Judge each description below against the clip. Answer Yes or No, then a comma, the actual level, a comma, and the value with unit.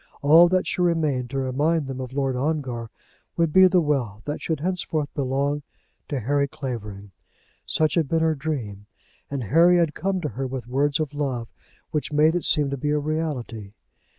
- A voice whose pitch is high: No, medium, 145 Hz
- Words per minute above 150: Yes, average, 185 wpm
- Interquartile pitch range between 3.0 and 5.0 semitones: Yes, average, 3.6 semitones